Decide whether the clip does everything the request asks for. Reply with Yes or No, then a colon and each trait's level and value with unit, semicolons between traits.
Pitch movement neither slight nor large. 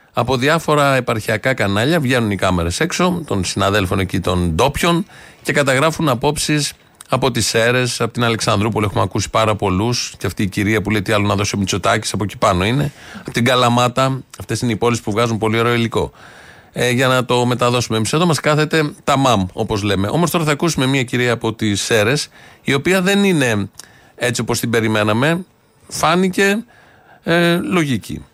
No: wide, 5.7 semitones